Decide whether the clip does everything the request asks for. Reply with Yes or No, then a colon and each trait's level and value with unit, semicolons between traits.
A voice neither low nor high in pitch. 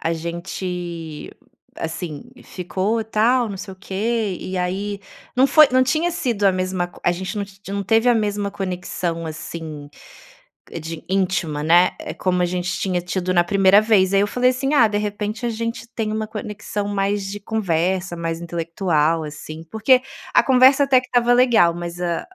No: high, 195 Hz